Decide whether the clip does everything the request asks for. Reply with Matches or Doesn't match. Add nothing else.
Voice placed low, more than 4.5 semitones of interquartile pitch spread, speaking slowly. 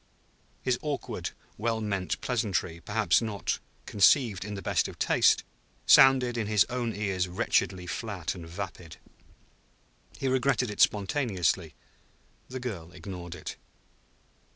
Matches